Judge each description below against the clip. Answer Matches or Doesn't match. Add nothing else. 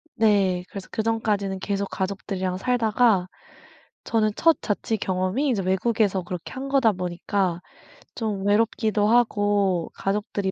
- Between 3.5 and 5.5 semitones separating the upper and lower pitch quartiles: Doesn't match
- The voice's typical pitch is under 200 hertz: Doesn't match